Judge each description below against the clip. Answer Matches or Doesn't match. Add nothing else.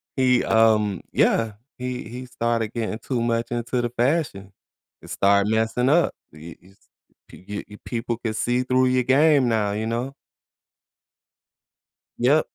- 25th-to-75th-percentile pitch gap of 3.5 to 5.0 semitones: Doesn't match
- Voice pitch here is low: Matches